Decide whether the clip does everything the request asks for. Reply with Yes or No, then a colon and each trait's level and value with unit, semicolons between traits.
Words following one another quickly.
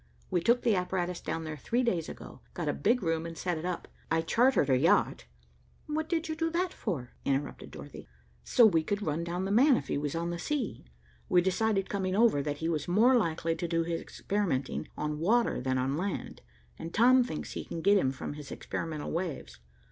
Yes: fast, 215 wpm